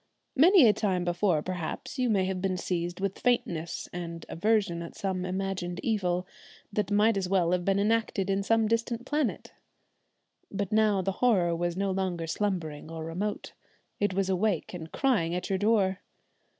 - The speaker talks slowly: No, average, 170 wpm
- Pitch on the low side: No, high, 190 Hz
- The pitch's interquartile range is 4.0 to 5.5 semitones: No, average, 3.1 semitones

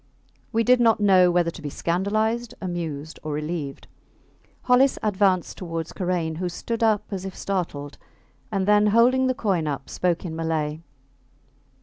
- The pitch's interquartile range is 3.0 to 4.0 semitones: No, average, 4.8 semitones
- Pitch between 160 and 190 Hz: Yes, medium, 185 Hz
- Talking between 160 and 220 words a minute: No, average, 150 wpm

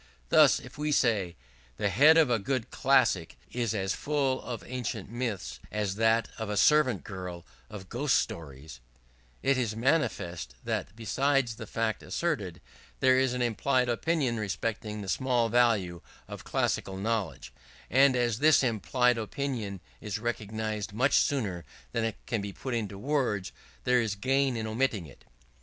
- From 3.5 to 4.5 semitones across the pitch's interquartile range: Yes, average, 4.2 semitones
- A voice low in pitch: Yes, low, 115 Hz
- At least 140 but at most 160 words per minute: Yes, average, 155 wpm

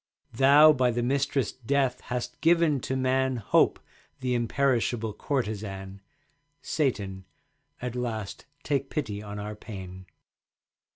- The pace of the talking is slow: Yes, slow, 115 wpm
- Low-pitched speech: Yes, low, 125 Hz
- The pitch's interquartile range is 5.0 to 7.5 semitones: No, average, 4.3 semitones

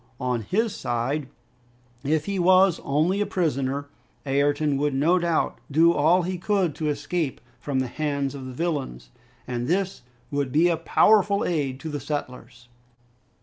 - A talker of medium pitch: Yes, medium, 150 Hz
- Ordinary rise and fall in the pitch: Yes, average, 4.4 semitones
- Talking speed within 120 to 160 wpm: Yes, average, 155 wpm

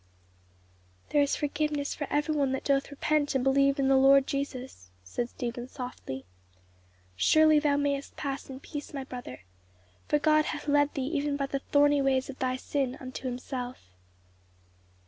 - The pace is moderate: Yes, average, 165 wpm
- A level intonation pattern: Yes, narrow, 2.0 semitones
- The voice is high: Yes, very high, 275 Hz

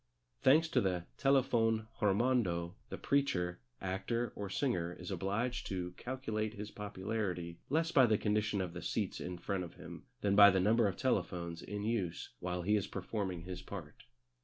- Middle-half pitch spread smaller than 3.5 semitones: No, average, 4.1 semitones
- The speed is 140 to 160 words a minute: No, average, 170 wpm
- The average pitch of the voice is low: Yes, low, 100 Hz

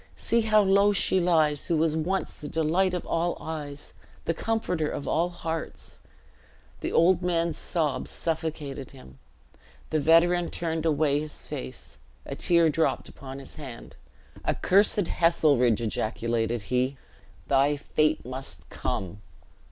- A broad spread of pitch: No, average, 3.8 semitones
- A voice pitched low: No, medium, 155 Hz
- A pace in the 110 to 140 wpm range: Yes, slow, 135 wpm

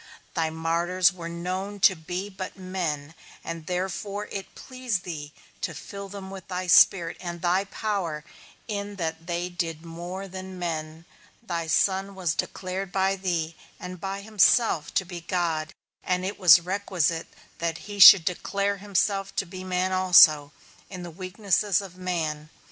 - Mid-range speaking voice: Yes, medium, 180 Hz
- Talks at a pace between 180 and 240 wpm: No, average, 155 wpm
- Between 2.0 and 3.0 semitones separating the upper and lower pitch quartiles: Yes, narrow, 2.5 semitones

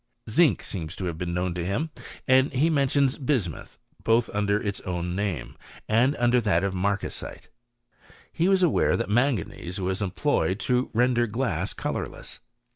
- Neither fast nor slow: Yes, average, 160 wpm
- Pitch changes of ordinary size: No, wide, 5.8 semitones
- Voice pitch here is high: No, low, 105 Hz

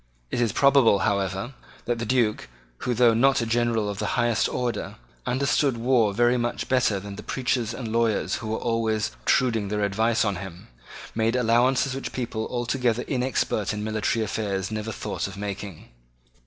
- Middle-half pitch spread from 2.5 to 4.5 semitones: Yes, average, 2.8 semitones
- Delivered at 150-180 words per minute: Yes, average, 170 wpm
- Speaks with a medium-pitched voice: No, low, 115 Hz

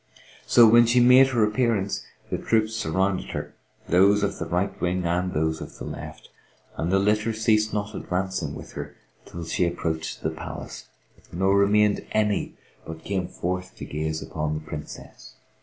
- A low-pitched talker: Yes, very low, 95 Hz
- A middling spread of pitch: Yes, average, 3.8 semitones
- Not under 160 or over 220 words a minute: Yes, average, 170 wpm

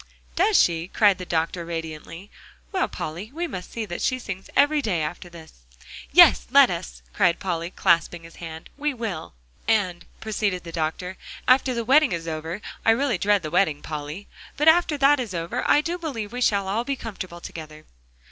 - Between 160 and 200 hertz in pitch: Yes, medium, 185 Hz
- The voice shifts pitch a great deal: Yes, wide, 6.6 semitones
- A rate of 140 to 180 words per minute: No, average, 190 wpm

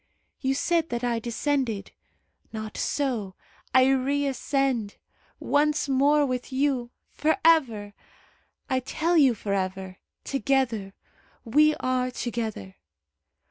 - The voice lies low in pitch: No, very high, 255 Hz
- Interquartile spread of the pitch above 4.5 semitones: No, average, 4.2 semitones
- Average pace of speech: No, slow, 105 wpm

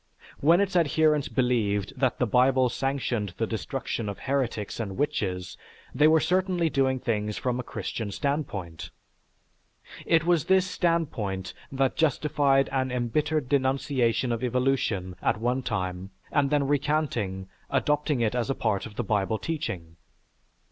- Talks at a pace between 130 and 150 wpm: Yes, average, 140 wpm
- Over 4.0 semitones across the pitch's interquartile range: Yes, wide, 5.4 semitones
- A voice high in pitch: No, low, 130 Hz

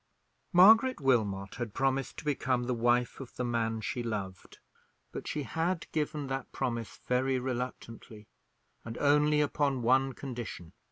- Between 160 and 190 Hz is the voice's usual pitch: No, low, 125 Hz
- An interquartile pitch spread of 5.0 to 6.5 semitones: No, average, 3.5 semitones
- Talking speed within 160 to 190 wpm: No, average, 145 wpm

